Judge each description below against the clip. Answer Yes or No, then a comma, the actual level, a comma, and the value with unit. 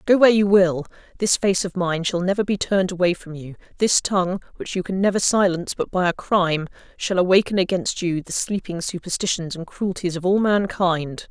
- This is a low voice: No, medium, 185 Hz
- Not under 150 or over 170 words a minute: No, average, 200 wpm